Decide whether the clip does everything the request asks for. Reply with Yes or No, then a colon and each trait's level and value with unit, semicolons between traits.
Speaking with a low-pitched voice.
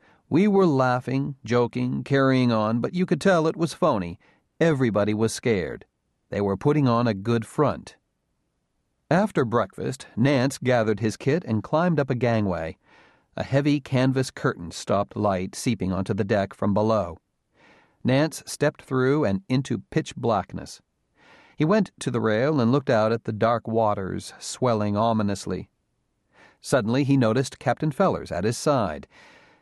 Yes: low, 125 Hz